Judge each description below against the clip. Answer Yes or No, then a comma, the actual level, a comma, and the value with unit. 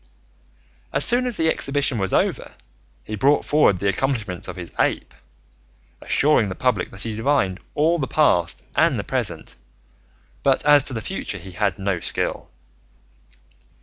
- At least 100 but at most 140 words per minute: No, average, 155 wpm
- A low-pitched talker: Yes, low, 115 Hz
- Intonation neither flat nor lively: No, wide, 7.1 semitones